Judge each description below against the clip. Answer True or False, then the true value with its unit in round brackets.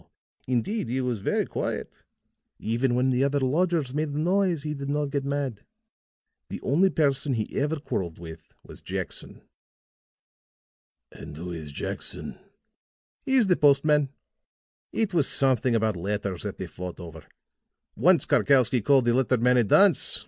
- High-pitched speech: False (135 Hz)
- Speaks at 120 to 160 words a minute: True (155 wpm)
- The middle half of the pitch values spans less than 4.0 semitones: False (4.7 semitones)